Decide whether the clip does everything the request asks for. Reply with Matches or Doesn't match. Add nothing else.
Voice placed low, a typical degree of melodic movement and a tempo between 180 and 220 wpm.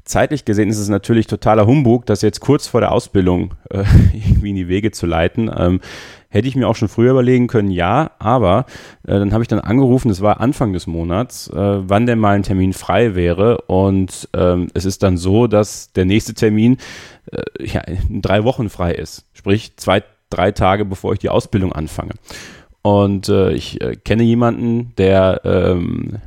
Matches